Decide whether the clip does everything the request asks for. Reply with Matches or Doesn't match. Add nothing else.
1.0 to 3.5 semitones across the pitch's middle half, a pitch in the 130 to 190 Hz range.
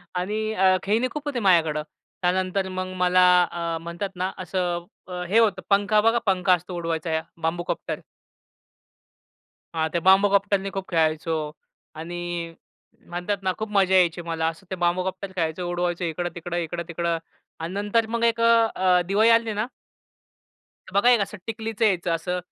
Matches